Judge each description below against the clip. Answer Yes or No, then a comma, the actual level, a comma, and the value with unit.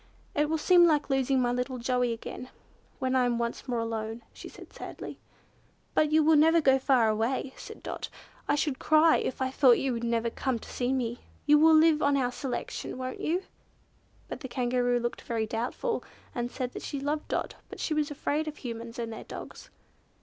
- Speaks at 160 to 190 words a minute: No, fast, 205 wpm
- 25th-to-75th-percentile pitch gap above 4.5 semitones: No, average, 3.8 semitones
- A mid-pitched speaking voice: No, very high, 260 Hz